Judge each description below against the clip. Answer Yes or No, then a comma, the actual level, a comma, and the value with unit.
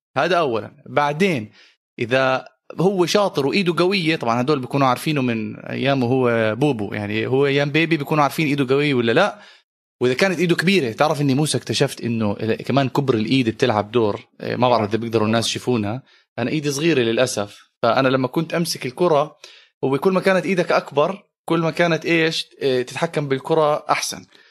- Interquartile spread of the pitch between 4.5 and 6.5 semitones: Yes, average, 4.8 semitones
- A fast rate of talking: Yes, fast, 165 wpm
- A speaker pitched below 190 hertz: Yes, medium, 140 Hz